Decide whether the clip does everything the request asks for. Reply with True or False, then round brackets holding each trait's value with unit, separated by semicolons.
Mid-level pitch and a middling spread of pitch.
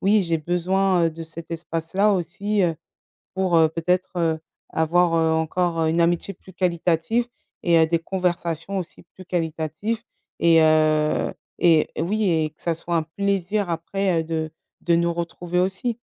False (170 Hz; 2.3 semitones)